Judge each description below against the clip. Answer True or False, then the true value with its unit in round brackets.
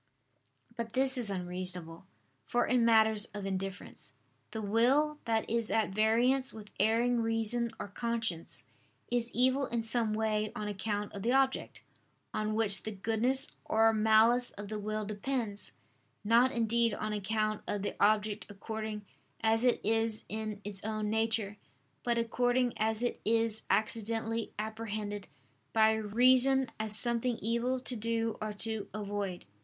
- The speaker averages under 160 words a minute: True (145 wpm)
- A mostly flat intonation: True (1.9 semitones)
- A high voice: True (220 Hz)